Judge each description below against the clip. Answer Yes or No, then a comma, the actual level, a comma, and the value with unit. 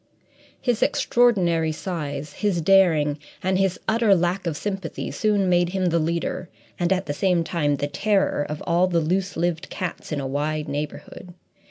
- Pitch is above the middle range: No, medium, 175 Hz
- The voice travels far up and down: No, average, 3.7 semitones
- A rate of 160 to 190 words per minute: Yes, average, 170 wpm